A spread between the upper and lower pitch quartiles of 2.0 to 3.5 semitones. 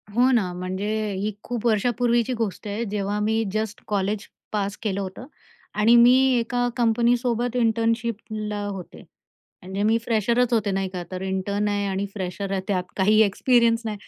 Yes: average, 2.8 semitones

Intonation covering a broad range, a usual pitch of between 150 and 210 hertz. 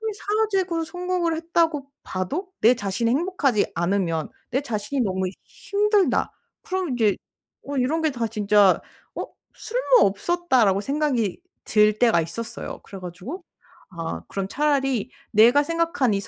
No: wide, 8.6 semitones; very high, 260 Hz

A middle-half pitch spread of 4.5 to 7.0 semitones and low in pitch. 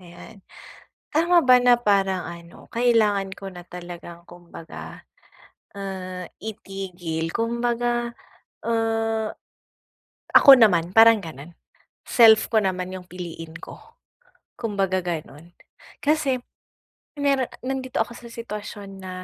No: average, 4.9 semitones; high, 200 Hz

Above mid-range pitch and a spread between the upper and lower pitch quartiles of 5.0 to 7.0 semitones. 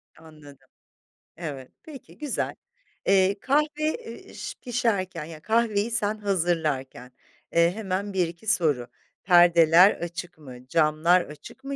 No: medium, 175 Hz; average, 5.3 semitones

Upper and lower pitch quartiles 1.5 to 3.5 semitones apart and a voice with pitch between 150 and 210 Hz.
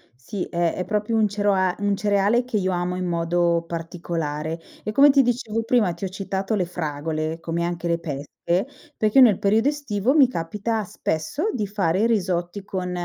No: average, 4.0 semitones; high, 190 Hz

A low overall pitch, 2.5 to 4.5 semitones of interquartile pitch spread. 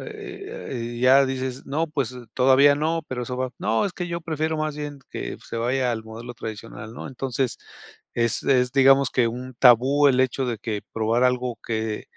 Yes: low, 130 Hz; average, 2.9 semitones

